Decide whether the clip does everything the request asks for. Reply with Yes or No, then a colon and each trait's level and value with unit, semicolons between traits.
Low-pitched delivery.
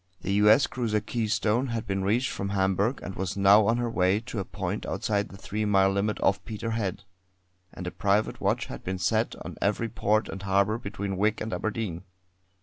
Yes: low, 105 Hz